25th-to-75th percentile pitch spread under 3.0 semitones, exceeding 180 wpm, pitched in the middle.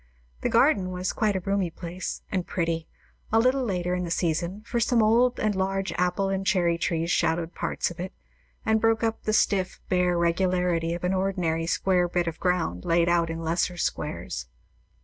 Yes: narrow, 2.4 semitones; average, 190 wpm; medium, 180 Hz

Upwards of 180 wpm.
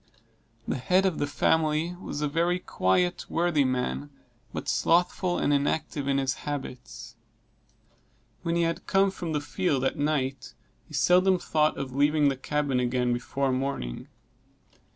No: average, 150 wpm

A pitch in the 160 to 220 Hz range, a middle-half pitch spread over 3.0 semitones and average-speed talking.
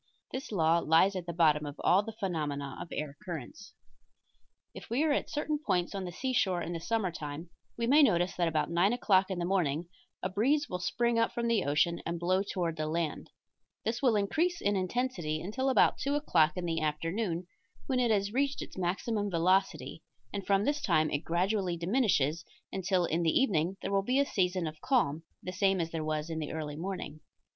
No: medium, 185 Hz; average, 5.1 semitones; fast, 210 wpm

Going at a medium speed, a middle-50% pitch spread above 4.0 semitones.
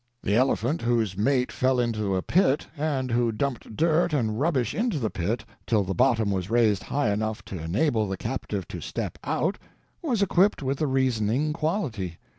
Yes: average, 175 wpm; wide, 5.5 semitones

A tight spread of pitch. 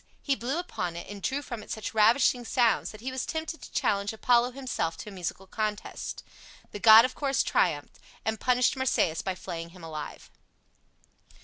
No: average, 5.2 semitones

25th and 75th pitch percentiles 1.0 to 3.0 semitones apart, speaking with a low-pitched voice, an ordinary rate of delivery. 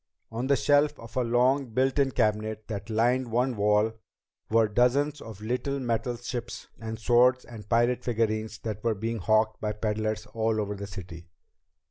Yes: narrow, 2.5 semitones; low, 115 Hz; average, 175 wpm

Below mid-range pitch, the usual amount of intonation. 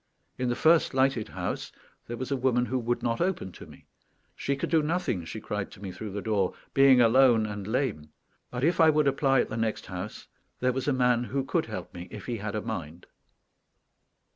Yes: low, 120 Hz; average, 4.3 semitones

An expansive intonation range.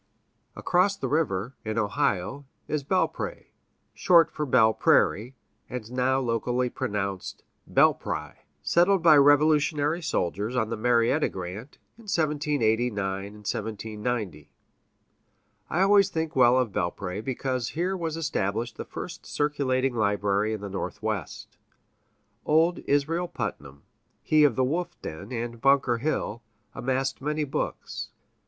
Yes: wide, 5.8 semitones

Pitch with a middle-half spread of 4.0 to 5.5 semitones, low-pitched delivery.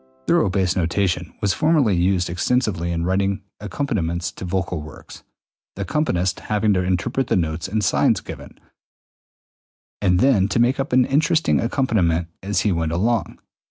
Yes: average, 4.9 semitones; very low, 95 Hz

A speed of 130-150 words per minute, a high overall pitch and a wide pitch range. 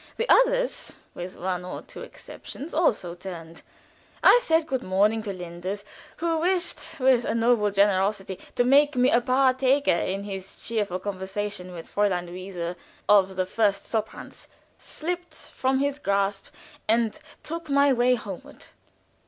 Yes: average, 145 wpm; high, 210 Hz; wide, 6.1 semitones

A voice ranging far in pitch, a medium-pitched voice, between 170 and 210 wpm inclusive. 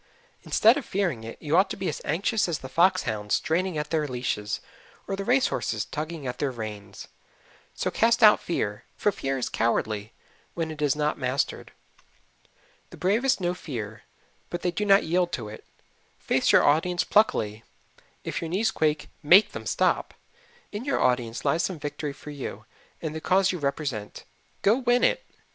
Yes: wide, 7.0 semitones; medium, 155 Hz; average, 180 wpm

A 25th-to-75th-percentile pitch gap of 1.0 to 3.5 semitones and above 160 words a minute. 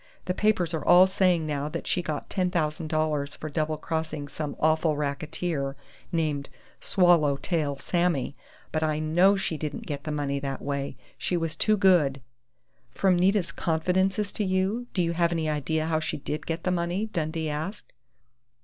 Yes: average, 3.1 semitones; average, 170 wpm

